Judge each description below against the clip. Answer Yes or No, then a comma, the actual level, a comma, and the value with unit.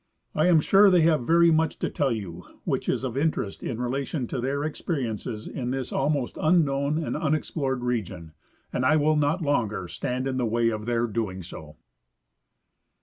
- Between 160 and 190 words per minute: Yes, average, 180 wpm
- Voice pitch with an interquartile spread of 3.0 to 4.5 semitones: No, average, 4.9 semitones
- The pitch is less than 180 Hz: Yes, low, 135 Hz